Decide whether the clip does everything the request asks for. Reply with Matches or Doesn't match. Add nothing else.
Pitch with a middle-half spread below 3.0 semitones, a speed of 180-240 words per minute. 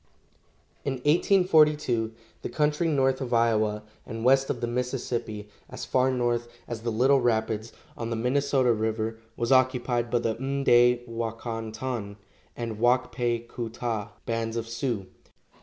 Doesn't match